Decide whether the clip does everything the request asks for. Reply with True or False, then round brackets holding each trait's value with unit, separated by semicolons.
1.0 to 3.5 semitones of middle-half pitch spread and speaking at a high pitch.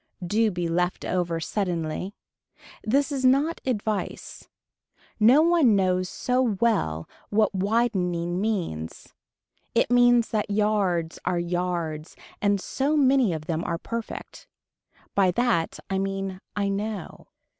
False (4.8 semitones; 200 Hz)